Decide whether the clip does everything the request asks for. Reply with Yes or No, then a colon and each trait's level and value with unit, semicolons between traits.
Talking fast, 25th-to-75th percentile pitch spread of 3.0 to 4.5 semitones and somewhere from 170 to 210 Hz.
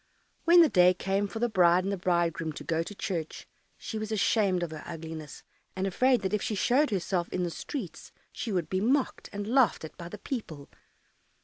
Yes: fast, 210 wpm; average, 4.1 semitones; high, 190 Hz